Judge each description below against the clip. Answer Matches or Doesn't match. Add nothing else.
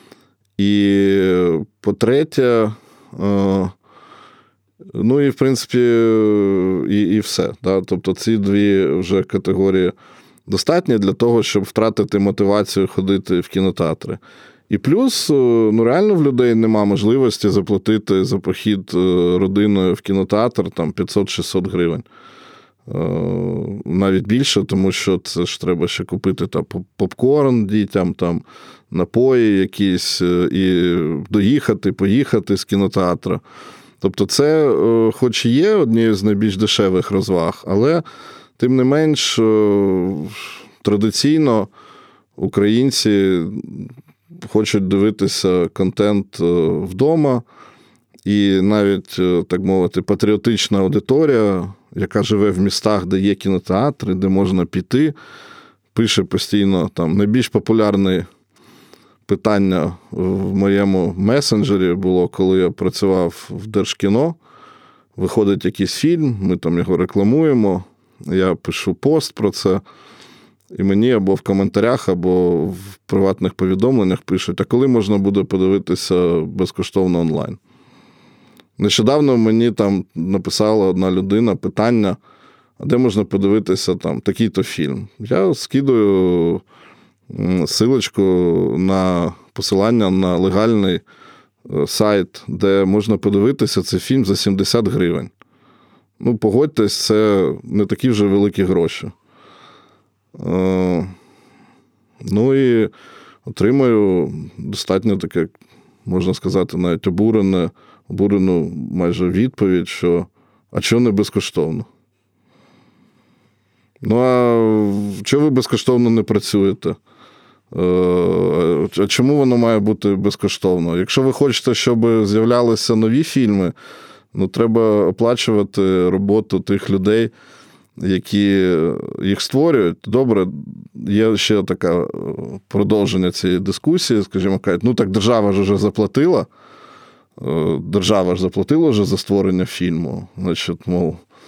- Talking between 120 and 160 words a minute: Doesn't match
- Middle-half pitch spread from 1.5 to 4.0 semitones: Matches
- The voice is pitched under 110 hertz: Matches